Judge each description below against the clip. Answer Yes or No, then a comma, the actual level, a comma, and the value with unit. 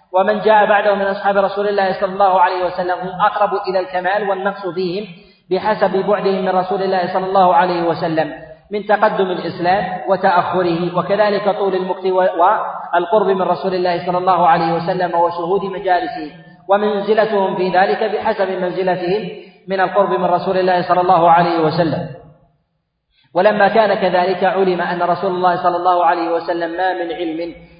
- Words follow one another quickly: Yes, fast, 155 wpm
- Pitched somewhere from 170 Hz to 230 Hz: Yes, medium, 185 Hz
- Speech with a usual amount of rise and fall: No, narrow, 2.0 semitones